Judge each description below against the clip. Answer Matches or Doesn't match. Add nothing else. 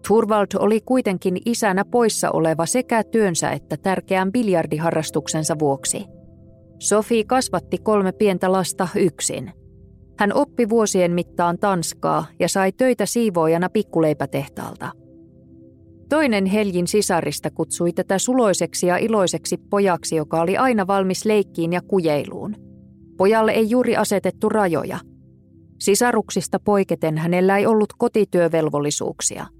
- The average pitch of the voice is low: Doesn't match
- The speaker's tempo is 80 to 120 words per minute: Matches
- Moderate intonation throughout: Matches